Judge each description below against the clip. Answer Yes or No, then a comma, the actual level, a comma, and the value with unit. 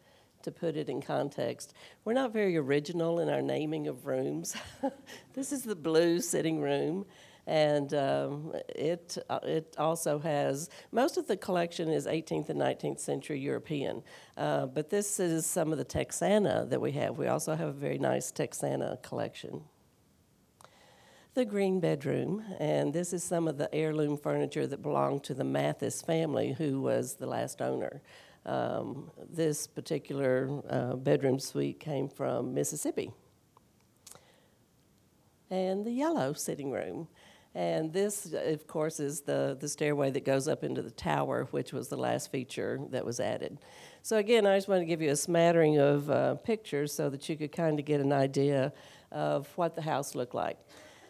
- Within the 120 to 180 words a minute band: Yes, average, 165 wpm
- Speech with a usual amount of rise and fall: Yes, average, 4.2 semitones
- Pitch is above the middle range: No, medium, 155 Hz